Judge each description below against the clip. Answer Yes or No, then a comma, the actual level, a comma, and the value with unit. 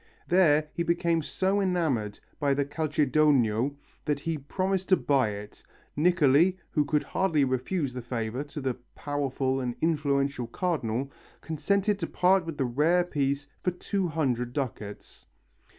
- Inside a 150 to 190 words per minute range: No, average, 140 wpm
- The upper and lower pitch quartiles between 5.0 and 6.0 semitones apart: No, average, 4.6 semitones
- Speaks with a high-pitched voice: No, medium, 145 Hz